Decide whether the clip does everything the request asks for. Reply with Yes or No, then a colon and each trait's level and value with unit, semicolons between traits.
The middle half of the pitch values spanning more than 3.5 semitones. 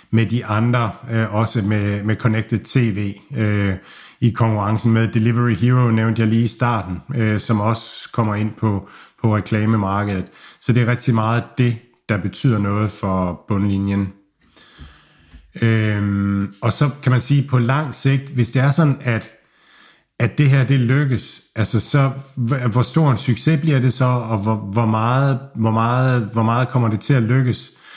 No: average, 2.8 semitones